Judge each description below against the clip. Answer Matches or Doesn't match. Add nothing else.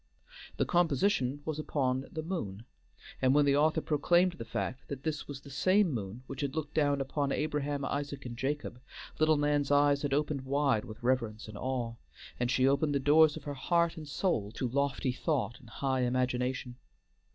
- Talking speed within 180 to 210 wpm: Matches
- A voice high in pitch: Doesn't match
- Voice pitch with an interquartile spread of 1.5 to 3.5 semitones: Matches